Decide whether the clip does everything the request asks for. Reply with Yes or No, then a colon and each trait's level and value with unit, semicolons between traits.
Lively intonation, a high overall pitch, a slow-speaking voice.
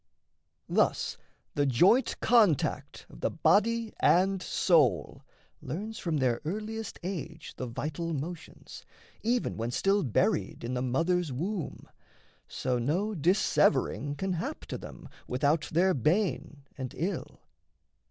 No: wide, 6.1 semitones; medium, 165 Hz; slow, 125 wpm